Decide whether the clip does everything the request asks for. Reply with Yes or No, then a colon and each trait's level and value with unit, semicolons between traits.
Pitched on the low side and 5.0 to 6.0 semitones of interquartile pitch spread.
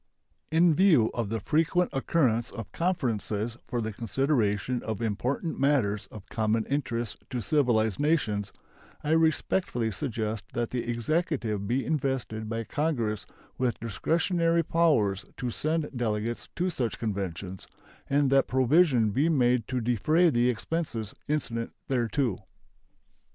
Yes: low, 120 Hz; wide, 5.5 semitones